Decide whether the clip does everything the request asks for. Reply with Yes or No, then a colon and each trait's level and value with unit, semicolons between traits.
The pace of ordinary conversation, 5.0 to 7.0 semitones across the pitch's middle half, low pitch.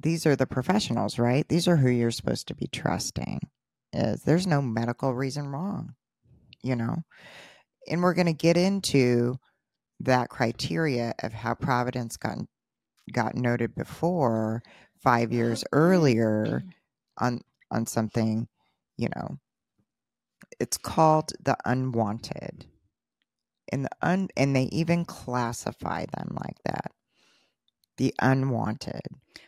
No: slow, 120 wpm; average, 5.3 semitones; low, 130 Hz